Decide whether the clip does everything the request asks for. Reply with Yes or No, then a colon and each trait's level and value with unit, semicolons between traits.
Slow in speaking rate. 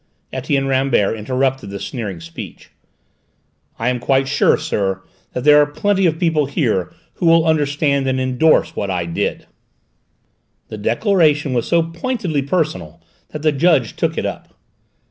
No: average, 150 wpm